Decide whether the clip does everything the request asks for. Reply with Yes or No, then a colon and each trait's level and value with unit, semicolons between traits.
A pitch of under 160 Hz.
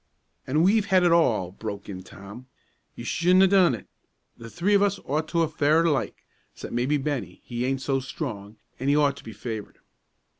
Yes: medium, 140 Hz